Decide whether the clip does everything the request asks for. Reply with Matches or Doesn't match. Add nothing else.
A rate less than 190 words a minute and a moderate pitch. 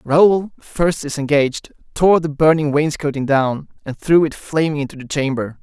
Matches